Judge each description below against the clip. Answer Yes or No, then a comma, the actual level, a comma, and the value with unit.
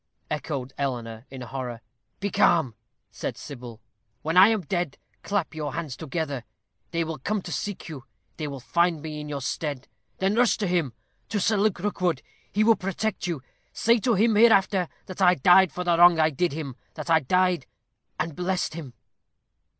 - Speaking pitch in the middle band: Yes, medium, 170 Hz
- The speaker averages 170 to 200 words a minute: Yes, average, 180 wpm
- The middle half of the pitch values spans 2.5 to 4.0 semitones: No, average, 5.2 semitones